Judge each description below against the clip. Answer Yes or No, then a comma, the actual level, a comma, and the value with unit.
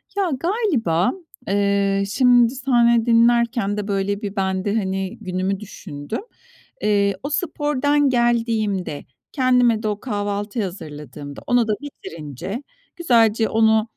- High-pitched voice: Yes, high, 215 Hz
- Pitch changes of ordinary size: Yes, average, 3.7 semitones